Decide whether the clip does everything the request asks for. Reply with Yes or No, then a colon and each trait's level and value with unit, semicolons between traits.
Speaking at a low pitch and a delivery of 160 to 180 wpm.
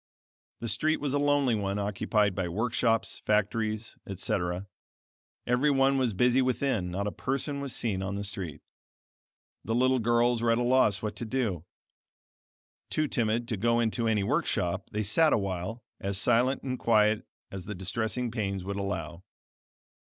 Yes: low, 110 Hz; average, 165 wpm